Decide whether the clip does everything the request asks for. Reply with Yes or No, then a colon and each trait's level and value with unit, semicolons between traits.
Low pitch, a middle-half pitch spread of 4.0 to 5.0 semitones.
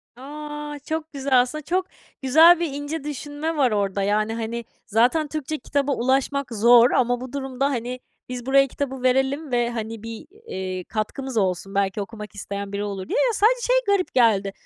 No: very high, 255 Hz; average, 4.7 semitones